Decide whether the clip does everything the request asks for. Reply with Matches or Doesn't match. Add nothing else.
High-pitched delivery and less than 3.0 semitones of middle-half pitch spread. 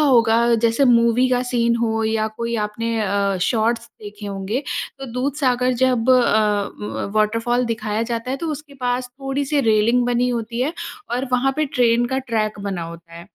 Matches